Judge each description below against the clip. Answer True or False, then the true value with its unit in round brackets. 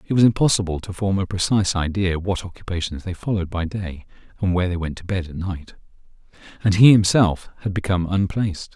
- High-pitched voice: False (95 Hz)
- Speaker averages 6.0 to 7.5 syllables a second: True (6.2 syllables/s)